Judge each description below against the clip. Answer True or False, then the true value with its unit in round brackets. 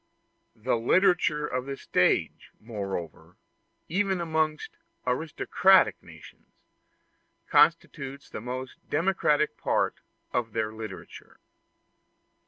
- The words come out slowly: True (85 wpm)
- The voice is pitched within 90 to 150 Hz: True (140 Hz)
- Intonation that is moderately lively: False (6.3 semitones)